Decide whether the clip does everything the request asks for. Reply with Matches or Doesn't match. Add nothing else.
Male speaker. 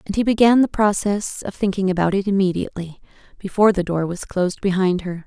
Doesn't match